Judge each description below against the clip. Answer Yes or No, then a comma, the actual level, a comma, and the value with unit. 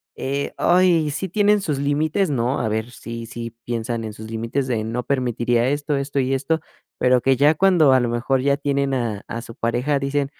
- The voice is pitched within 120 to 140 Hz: Yes, low, 135 Hz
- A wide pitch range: No, average, 3.5 semitones